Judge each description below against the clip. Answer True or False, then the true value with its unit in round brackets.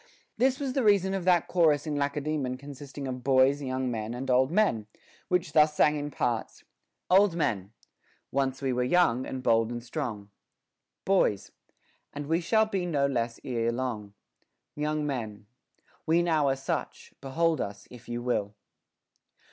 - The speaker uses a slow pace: False (165 wpm)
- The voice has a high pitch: False (140 Hz)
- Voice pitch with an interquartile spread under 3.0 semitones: False (4.8 semitones)